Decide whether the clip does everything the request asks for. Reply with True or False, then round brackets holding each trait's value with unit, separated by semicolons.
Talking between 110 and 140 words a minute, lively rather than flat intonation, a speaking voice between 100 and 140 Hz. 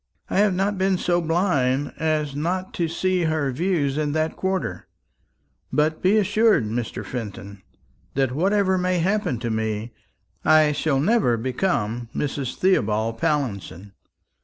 False (135 wpm; 7.0 semitones; 155 Hz)